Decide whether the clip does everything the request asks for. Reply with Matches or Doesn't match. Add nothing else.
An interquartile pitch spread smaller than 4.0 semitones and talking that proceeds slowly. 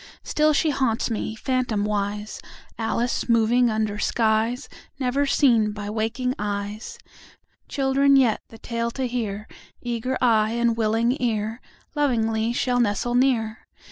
Matches